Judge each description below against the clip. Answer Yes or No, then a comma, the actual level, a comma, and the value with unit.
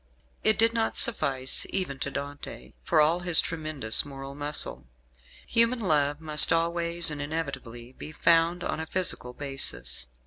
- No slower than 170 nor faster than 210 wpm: No, average, 145 wpm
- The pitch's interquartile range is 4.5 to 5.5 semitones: No, average, 3.6 semitones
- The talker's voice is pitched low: No, medium, 155 Hz